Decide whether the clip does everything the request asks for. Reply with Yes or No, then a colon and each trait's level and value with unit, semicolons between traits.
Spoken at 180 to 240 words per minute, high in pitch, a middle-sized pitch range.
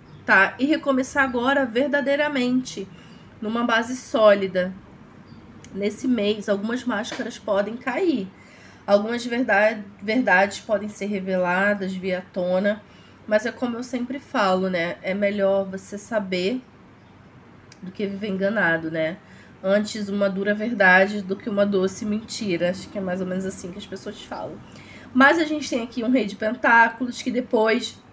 No: average, 145 wpm; high, 210 Hz; average, 3.8 semitones